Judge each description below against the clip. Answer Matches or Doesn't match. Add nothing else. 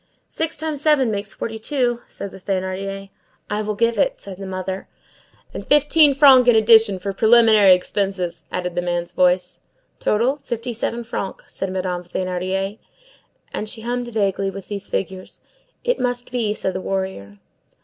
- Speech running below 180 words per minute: Matches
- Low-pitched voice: Doesn't match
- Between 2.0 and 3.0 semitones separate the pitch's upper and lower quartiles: Doesn't match